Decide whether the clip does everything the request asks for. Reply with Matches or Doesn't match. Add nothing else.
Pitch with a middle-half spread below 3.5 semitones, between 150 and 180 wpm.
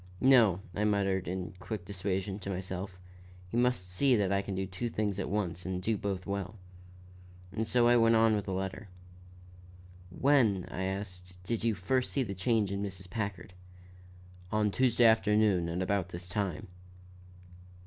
Matches